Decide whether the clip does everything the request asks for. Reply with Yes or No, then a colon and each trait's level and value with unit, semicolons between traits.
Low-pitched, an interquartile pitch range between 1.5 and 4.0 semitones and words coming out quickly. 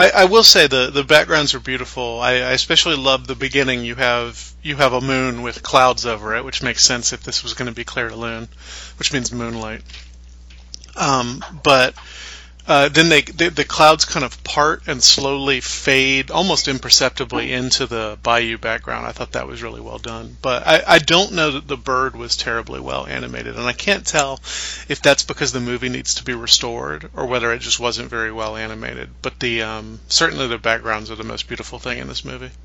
Yes: low, 125 Hz; average, 3.6 semitones; fast, 210 wpm